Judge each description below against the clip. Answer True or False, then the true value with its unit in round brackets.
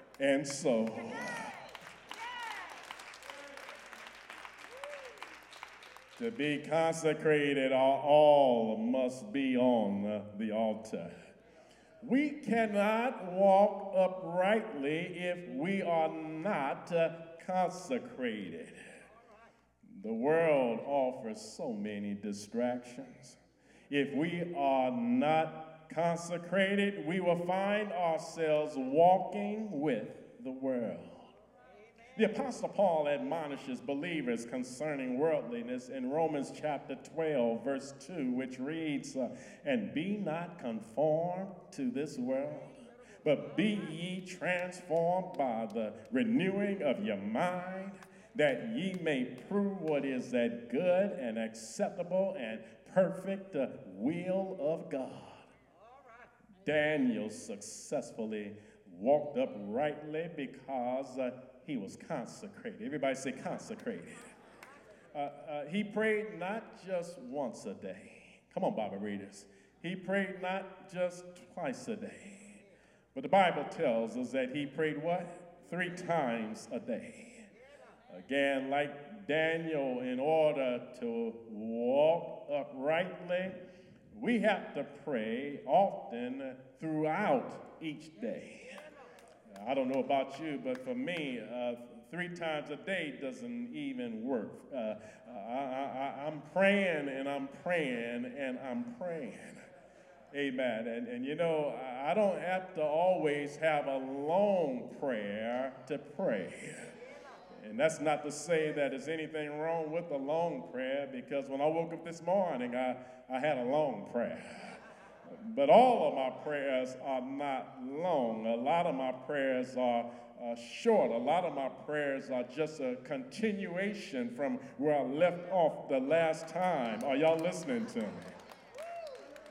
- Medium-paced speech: False (120 wpm)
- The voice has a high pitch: False (165 Hz)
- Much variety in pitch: True (6.8 semitones)